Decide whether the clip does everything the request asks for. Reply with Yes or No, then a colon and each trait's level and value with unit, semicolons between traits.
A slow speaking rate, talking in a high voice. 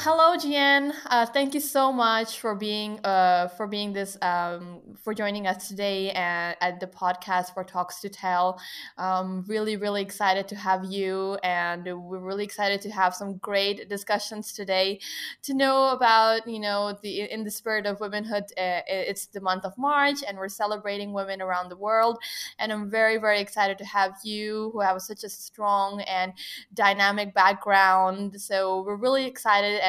No: average, 175 wpm; high, 200 Hz